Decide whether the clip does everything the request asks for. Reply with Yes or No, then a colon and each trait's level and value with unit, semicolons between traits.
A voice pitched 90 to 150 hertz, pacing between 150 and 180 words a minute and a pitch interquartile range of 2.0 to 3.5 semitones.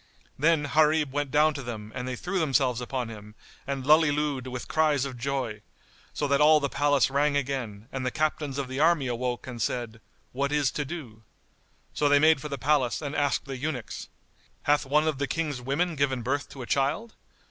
No: medium, 140 Hz; average, 200 wpm; average, 2.8 semitones